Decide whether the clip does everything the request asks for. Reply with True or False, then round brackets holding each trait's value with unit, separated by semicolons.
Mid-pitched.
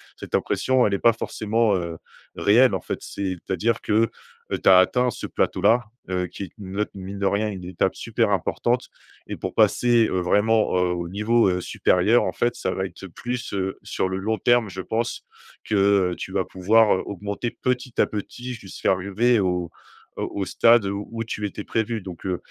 False (100 Hz)